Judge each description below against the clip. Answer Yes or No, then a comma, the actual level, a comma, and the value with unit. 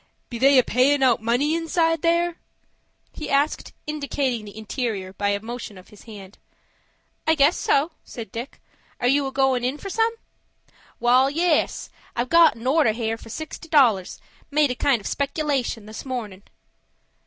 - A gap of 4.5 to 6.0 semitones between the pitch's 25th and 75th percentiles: Yes, average, 4.9 semitones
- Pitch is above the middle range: Yes, very high, 260 Hz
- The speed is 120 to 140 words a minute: No, average, 165 wpm